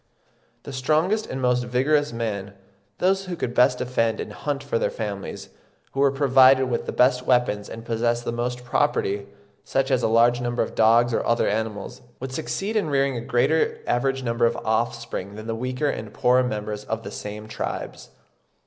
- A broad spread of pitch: No, average, 2.9 semitones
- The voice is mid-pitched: No, low, 120 Hz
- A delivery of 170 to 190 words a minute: Yes, average, 180 wpm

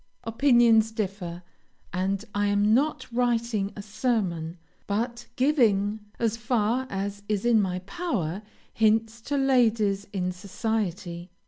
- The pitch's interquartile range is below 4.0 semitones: Yes, average, 3.2 semitones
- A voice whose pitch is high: Yes, high, 215 Hz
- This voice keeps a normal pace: No, slow, 120 wpm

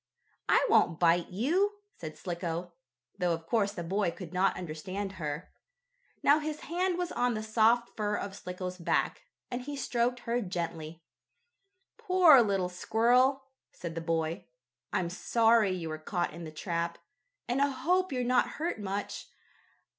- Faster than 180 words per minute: No, average, 155 wpm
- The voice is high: Yes, high, 200 Hz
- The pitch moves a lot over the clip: Yes, wide, 6.4 semitones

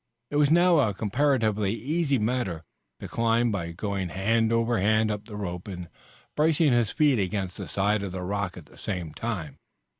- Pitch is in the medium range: No, low, 105 Hz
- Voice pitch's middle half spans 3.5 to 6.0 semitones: Yes, average, 4.1 semitones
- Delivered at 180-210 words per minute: Yes, average, 185 wpm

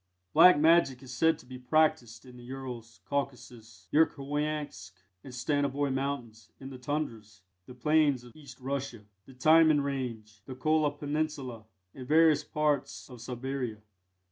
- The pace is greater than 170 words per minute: No, average, 145 wpm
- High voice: No, low, 135 Hz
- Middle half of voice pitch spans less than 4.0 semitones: Yes, average, 3.3 semitones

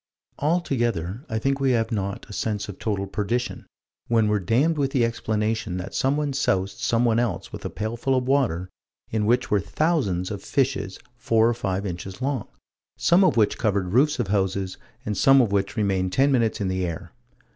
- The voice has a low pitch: Yes, low, 110 Hz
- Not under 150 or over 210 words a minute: Yes, average, 190 wpm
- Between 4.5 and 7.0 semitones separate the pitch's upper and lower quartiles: Yes, average, 4.8 semitones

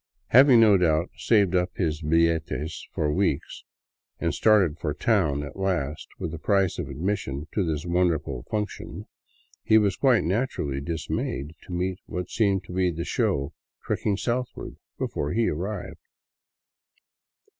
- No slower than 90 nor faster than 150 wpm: Yes, average, 145 wpm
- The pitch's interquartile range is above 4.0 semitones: Yes, average, 4.8 semitones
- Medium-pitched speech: No, very low, 90 Hz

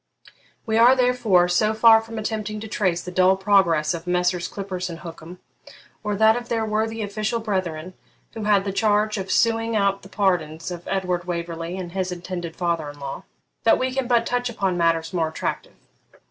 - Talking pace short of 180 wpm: No, average, 190 wpm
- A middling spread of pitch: Yes, average, 3.9 semitones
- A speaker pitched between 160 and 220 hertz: Yes, high, 190 Hz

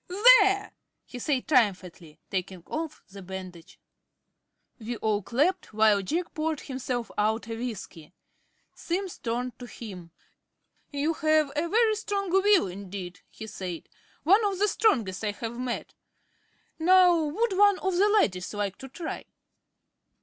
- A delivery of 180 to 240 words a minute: No, average, 140 wpm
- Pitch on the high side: Yes, very high, 255 Hz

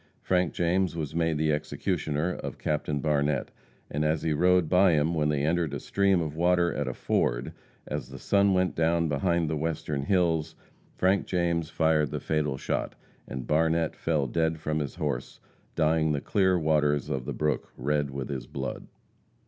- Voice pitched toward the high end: No, very low, 80 Hz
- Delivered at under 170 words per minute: No, average, 180 wpm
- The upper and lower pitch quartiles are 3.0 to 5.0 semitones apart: No, narrow, 2.6 semitones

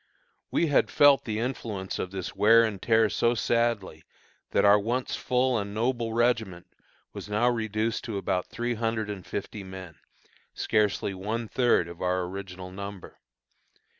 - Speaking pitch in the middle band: No, low, 110 Hz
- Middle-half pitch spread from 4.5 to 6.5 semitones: No, average, 3.5 semitones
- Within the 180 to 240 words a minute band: No, average, 155 wpm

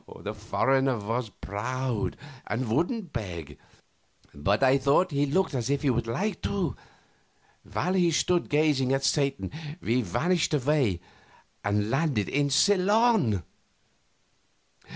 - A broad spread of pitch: Yes, wide, 6.3 semitones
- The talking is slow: Yes, slow, 125 wpm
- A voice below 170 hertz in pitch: Yes, low, 135 Hz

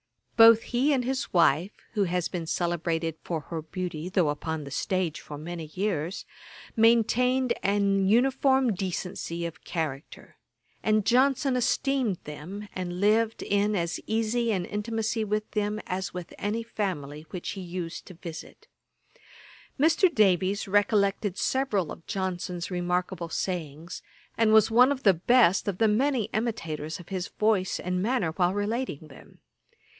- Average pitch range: Yes, average, 4.5 semitones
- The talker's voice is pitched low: No, high, 195 Hz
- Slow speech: No, average, 145 wpm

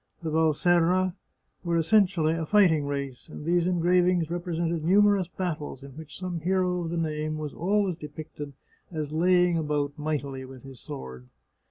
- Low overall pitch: No, medium, 165 Hz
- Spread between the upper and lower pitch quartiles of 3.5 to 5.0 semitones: No, average, 3.1 semitones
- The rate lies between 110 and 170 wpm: Yes, average, 155 wpm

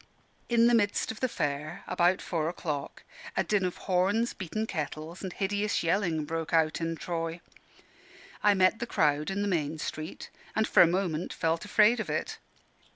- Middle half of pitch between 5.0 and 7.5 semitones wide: No, average, 4.2 semitones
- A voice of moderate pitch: Yes, medium, 175 Hz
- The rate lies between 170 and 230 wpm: Yes, average, 175 wpm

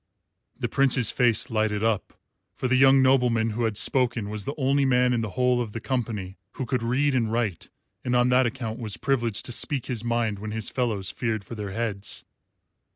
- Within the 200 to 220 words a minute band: Yes, fast, 205 wpm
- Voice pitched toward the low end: Yes, low, 120 Hz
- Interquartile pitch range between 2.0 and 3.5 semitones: Yes, average, 2.7 semitones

